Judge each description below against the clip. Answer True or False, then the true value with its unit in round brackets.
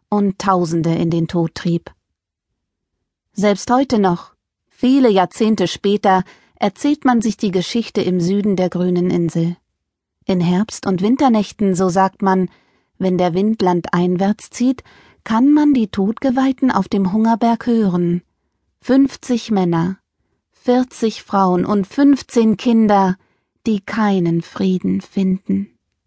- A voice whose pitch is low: False (200 Hz)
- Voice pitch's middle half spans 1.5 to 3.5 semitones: False (4.2 semitones)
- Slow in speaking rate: True (120 wpm)